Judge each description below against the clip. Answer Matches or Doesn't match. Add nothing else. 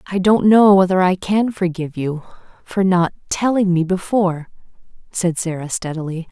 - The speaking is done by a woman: Matches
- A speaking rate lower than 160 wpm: Matches